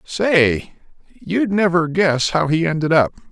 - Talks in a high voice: No, medium, 165 Hz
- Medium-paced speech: Yes, average, 145 wpm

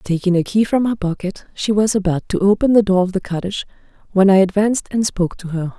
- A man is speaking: No, female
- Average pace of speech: No, fast, 240 wpm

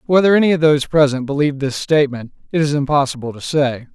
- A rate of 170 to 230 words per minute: Yes, average, 200 wpm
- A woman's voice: No, male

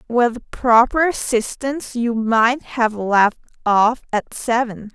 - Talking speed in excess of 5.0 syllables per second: No, 3.4 syllables/s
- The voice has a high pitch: Yes, high, 235 Hz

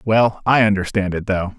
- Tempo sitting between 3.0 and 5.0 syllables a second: Yes, 4.9 syllables/s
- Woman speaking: No, male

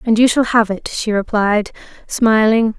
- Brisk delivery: No, average, 170 wpm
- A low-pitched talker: No, high, 220 Hz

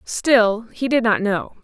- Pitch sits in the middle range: No, high, 230 Hz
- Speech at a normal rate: Yes, average, 185 wpm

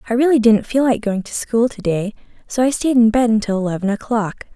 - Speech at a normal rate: No, fast, 235 wpm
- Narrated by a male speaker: No, female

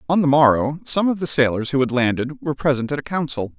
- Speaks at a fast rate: Yes, fast, 250 wpm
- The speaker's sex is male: Yes, male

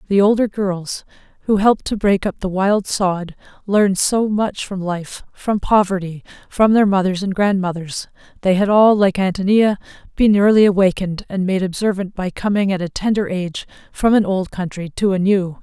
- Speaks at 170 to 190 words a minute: Yes, average, 180 wpm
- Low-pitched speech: No, high, 195 Hz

